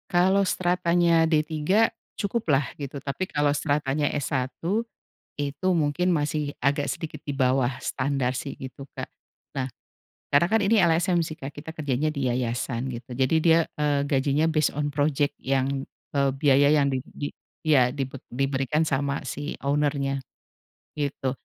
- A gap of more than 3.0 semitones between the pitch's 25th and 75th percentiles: No, narrow, 2.5 semitones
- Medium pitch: Yes, medium, 145 Hz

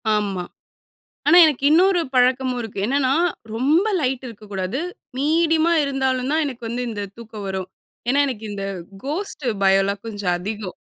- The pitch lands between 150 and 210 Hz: No, very high, 250 Hz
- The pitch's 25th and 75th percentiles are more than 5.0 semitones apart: Yes, wide, 5.6 semitones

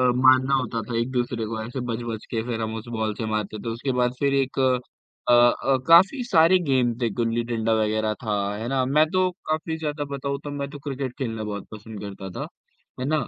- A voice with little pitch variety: No, average, 3.6 semitones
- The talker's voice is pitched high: No, low, 120 Hz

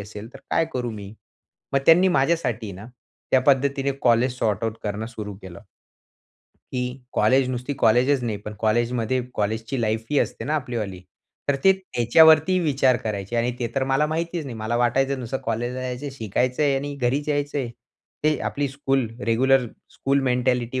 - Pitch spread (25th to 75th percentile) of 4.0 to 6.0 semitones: No, average, 3.5 semitones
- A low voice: Yes, low, 125 Hz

